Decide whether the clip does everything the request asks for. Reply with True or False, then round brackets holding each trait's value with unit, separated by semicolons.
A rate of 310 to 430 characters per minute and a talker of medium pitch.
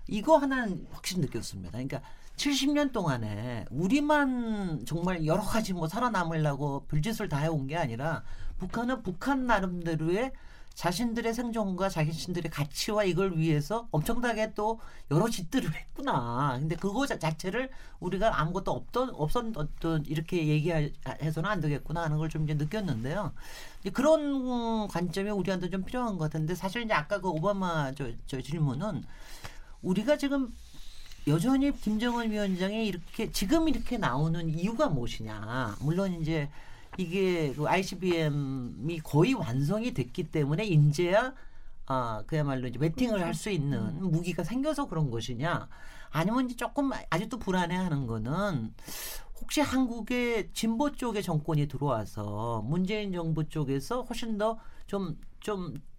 True (315 characters per minute; 175 Hz)